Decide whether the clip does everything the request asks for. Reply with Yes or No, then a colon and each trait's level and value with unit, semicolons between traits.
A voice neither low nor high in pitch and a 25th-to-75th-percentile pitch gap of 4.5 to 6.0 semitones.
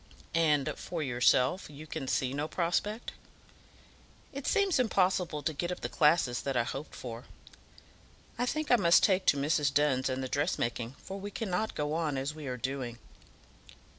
Yes: medium, 150 Hz; wide, 5.4 semitones